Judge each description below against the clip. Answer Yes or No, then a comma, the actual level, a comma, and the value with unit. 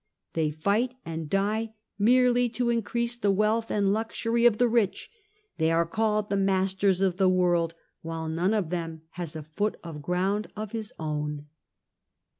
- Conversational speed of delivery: Yes, average, 165 wpm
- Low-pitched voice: No, high, 195 Hz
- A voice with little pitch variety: No, average, 5.0 semitones